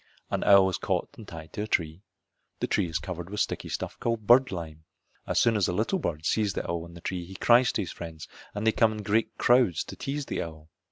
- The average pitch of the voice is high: No, very low, 95 Hz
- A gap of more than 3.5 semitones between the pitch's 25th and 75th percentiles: Yes, average, 4.9 semitones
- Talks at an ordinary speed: No, fast, 255 wpm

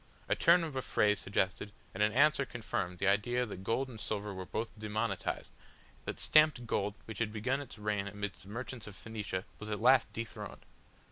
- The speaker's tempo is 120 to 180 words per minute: No, average, 195 wpm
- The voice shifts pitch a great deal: No, average, 3.4 semitones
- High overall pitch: No, low, 110 Hz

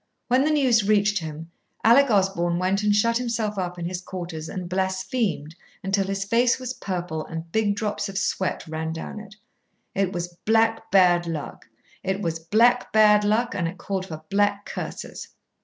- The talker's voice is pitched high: Yes, high, 195 Hz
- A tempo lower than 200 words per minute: Yes, average, 175 wpm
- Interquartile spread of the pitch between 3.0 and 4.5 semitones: Yes, average, 3.7 semitones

